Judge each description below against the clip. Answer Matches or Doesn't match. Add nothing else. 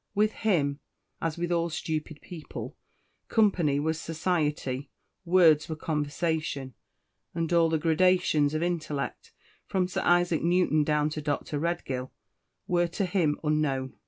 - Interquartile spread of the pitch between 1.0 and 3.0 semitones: Matches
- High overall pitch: Doesn't match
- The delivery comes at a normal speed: Doesn't match